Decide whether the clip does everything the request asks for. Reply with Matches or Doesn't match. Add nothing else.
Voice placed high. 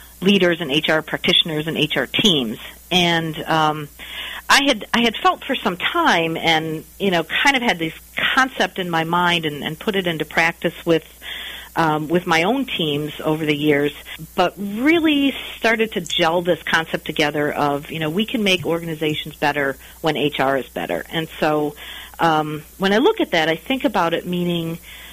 Doesn't match